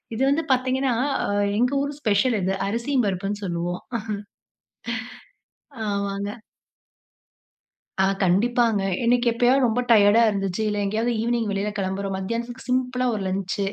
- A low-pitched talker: No, high, 220 Hz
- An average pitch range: Yes, average, 3.8 semitones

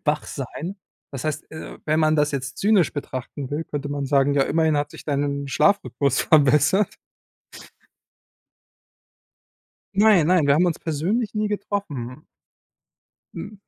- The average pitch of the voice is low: No, medium, 150 Hz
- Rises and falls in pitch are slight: No, average, 4.2 semitones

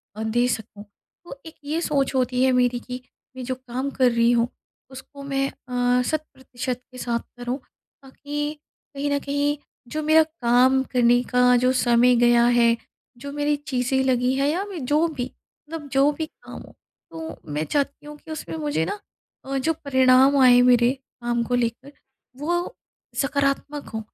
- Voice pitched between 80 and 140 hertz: No, very high, 260 Hz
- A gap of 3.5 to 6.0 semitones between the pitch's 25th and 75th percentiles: No, average, 2.9 semitones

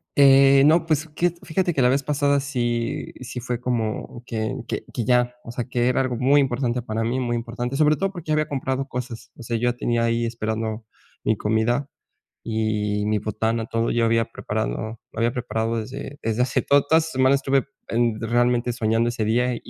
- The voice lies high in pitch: No, low, 120 Hz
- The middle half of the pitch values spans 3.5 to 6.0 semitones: No, average, 3.0 semitones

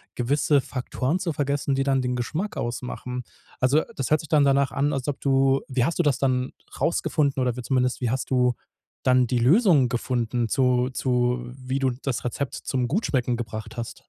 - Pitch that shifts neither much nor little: No, narrow, 2.1 semitones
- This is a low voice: Yes, low, 130 Hz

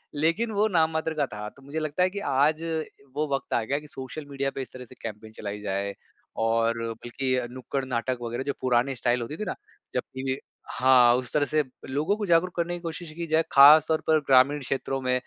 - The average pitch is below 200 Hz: Yes, low, 135 Hz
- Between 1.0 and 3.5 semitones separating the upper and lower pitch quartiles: No, average, 4.1 semitones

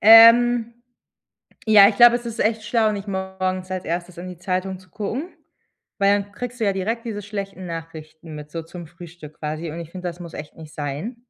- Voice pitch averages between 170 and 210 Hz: Yes, high, 190 Hz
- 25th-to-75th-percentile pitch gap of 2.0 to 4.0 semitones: No, average, 4.5 semitones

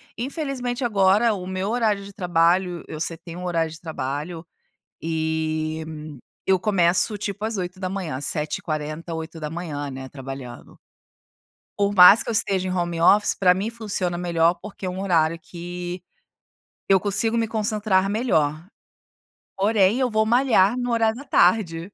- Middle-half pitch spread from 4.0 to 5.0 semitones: Yes, average, 4.3 semitones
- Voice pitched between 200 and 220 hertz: No, medium, 185 Hz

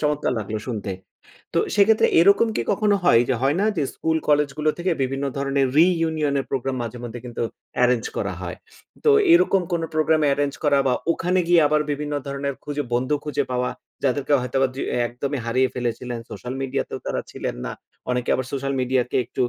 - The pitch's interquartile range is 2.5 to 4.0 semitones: Yes, average, 3.7 semitones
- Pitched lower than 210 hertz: Yes, medium, 140 Hz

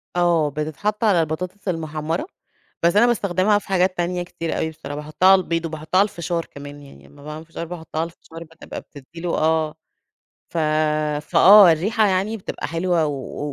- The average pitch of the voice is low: No, medium, 165 Hz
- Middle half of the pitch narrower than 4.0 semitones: Yes, average, 3.0 semitones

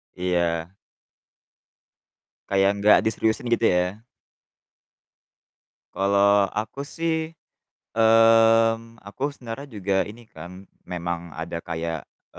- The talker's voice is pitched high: No, low, 100 Hz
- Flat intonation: No, average, 4.1 semitones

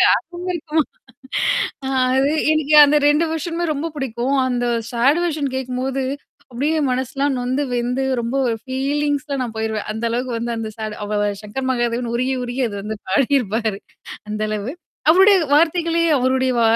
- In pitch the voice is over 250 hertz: Yes, very high, 260 Hz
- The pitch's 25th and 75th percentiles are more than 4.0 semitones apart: No, average, 3.7 semitones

